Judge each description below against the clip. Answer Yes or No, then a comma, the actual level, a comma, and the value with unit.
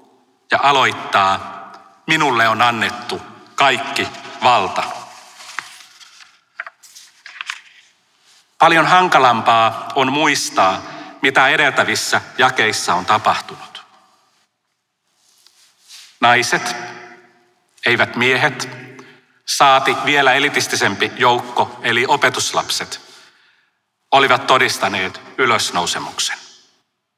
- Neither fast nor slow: No, slow, 60 wpm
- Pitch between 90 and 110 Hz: No, low, 120 Hz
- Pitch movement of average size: No, narrow, 2.3 semitones